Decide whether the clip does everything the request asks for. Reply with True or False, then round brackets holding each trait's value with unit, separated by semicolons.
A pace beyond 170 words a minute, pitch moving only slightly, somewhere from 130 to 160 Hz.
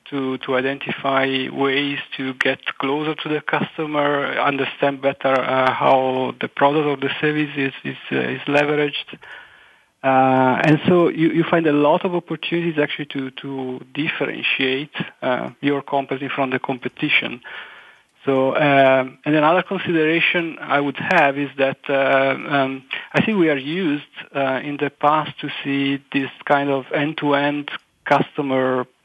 False (155 wpm; 2.1 semitones; 140 Hz)